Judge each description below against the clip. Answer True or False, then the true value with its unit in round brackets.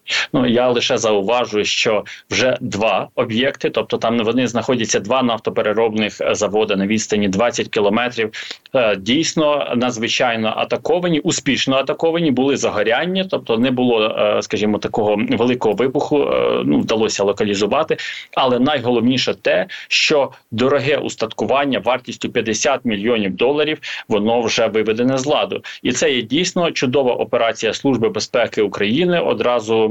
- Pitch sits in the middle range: False (120 Hz)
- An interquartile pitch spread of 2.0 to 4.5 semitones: False (5.5 semitones)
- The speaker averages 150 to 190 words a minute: False (120 wpm)